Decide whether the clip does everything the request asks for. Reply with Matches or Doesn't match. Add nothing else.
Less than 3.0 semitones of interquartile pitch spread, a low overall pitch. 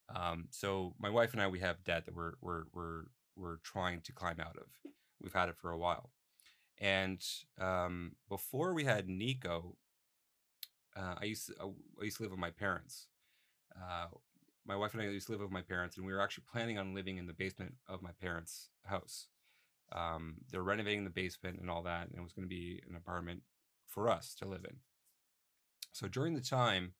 Matches